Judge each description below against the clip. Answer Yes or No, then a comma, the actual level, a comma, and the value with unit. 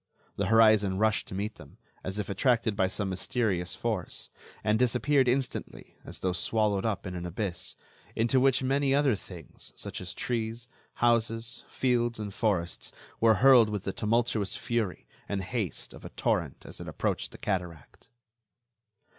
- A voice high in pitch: No, low, 110 Hz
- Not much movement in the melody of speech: No, average, 3.9 semitones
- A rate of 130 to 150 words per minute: No, average, 160 wpm